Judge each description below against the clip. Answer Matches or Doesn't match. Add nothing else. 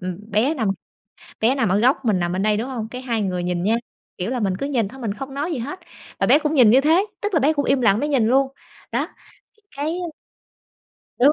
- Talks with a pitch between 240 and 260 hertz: Matches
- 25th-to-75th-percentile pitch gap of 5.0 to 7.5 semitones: Matches